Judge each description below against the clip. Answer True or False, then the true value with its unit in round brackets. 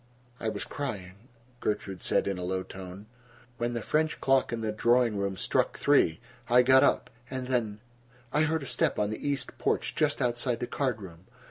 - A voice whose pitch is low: True (120 Hz)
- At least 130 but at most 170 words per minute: False (190 wpm)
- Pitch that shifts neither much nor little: True (4.4 semitones)